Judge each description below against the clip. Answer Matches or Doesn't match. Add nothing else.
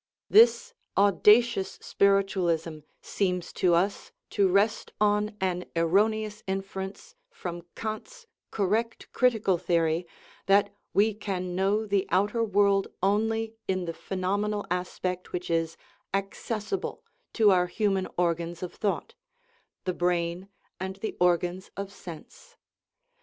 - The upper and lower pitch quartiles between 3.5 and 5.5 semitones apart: Doesn't match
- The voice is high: Matches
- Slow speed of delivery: Matches